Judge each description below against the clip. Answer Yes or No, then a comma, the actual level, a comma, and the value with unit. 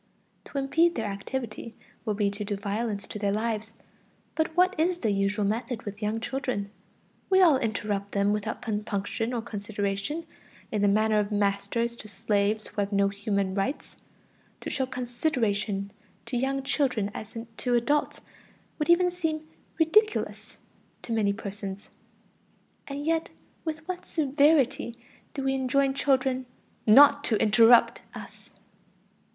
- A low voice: No, high, 230 Hz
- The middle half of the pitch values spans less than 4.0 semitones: No, average, 5.2 semitones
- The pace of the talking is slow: No, average, 145 wpm